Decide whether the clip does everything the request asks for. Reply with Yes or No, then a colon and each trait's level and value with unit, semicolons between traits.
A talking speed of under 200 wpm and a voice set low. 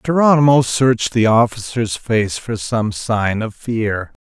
Yes: average, 140 wpm; low, 120 Hz